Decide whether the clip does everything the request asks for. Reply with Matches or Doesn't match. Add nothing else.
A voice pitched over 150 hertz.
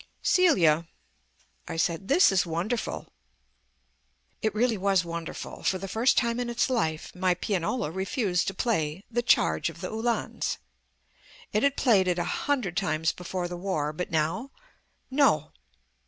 Matches